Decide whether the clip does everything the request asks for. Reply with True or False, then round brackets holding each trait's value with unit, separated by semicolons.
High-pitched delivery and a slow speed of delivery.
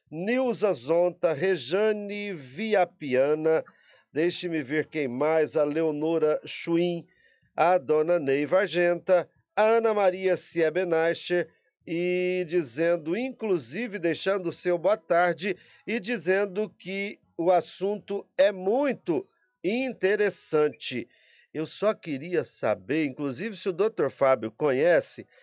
False (175 Hz; 105 wpm)